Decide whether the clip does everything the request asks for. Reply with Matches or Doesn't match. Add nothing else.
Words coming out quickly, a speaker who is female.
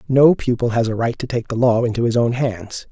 Doesn't match